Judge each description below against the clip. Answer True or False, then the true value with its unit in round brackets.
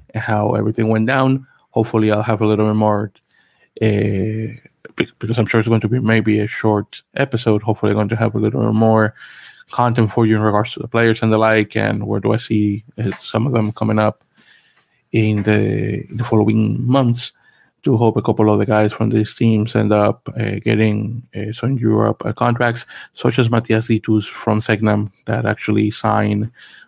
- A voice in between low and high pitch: False (110 Hz)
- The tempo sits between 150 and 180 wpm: False (190 wpm)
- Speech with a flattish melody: True (1.4 semitones)